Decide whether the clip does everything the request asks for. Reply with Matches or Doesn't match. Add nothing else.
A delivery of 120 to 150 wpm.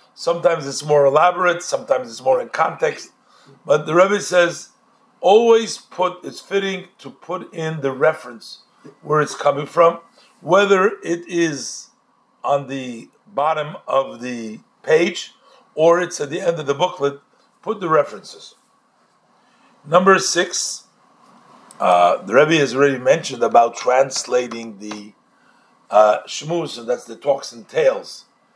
Matches